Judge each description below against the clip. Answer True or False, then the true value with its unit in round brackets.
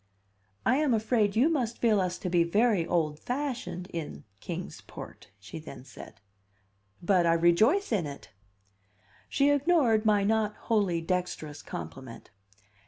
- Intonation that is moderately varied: False (5.8 semitones)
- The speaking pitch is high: True (195 Hz)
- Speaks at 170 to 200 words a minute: False (140 wpm)